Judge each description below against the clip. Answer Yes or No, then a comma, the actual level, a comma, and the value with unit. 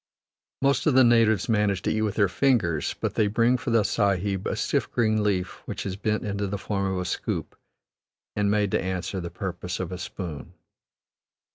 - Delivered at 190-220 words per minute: Yes, average, 195 wpm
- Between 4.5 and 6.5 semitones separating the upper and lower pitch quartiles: No, average, 2.8 semitones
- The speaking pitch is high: No, low, 100 Hz